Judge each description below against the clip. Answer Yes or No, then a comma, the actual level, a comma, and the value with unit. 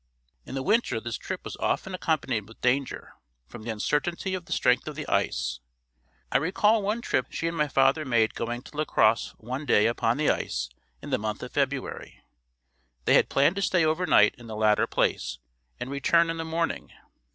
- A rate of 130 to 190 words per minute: No, average, 200 wpm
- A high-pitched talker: No, low, 135 Hz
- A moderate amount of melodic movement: No, wide, 6.3 semitones